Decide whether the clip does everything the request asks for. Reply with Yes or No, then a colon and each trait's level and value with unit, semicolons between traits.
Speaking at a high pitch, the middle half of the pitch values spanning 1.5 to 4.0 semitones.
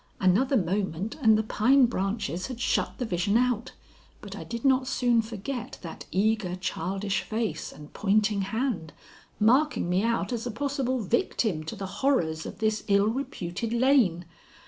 No: high, 220 Hz; average, 4.4 semitones